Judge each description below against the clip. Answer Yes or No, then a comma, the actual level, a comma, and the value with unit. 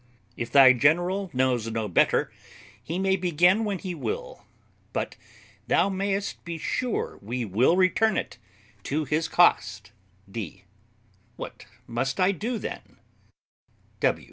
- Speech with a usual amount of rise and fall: No, wide, 7.7 semitones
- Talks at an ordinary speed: No, slow, 125 wpm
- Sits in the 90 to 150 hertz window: No, medium, 170 Hz